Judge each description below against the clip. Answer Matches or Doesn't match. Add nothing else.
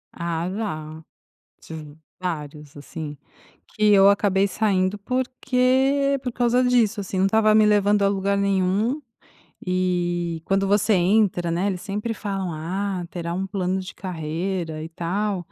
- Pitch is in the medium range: Doesn't match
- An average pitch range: Matches